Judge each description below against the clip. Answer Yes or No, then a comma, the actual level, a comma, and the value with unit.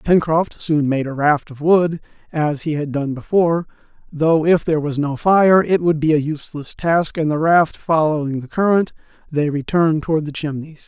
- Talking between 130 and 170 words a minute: No, average, 195 wpm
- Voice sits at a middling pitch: Yes, medium, 155 Hz